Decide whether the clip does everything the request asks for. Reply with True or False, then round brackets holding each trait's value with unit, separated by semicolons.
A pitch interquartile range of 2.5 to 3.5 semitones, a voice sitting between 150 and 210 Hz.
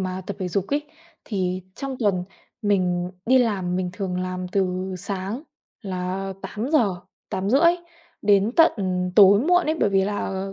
True (2.8 semitones; 195 Hz)